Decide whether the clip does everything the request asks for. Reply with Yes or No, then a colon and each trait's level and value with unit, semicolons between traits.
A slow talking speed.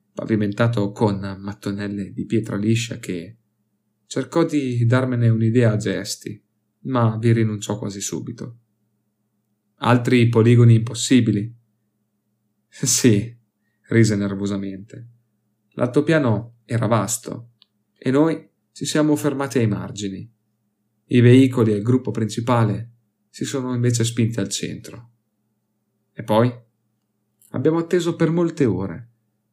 Yes: slow, 110 wpm